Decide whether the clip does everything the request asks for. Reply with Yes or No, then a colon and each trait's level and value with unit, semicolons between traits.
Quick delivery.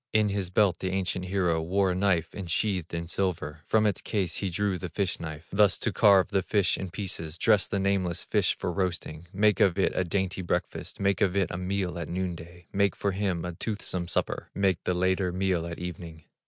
Yes: fast, 215 wpm